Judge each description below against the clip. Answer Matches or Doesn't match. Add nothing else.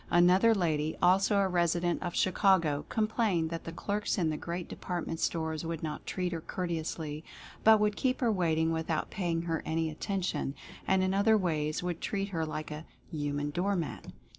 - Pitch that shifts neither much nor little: Matches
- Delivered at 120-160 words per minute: Doesn't match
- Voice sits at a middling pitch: Matches